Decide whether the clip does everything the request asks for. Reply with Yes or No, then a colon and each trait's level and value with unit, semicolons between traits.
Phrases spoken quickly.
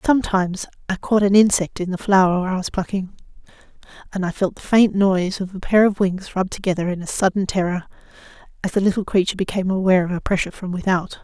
Yes: fast, 210 wpm